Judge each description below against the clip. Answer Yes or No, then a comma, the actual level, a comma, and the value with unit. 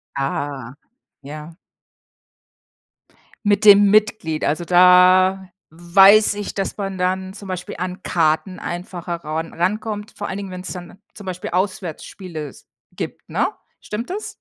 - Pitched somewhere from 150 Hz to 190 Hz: Yes, medium, 185 Hz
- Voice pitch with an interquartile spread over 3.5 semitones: No, average, 2.9 semitones